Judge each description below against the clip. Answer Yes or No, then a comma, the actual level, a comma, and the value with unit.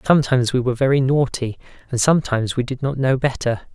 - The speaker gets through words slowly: No, average, 190 wpm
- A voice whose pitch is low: Yes, low, 130 Hz